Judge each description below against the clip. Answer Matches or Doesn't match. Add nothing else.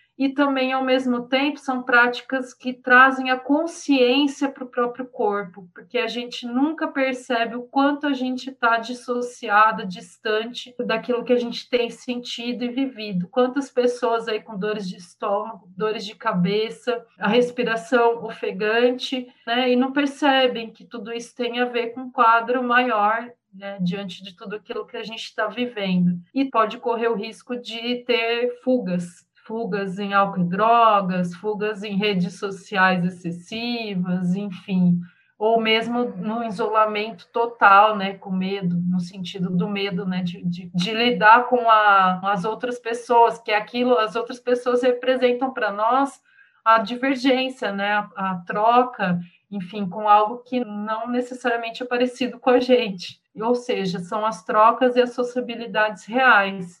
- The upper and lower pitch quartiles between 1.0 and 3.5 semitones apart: Matches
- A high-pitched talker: Matches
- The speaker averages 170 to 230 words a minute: Doesn't match